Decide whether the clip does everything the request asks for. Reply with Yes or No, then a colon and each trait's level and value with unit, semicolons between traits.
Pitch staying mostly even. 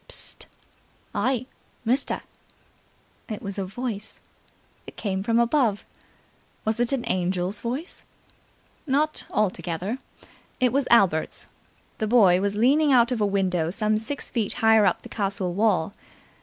No: average, 4.1 semitones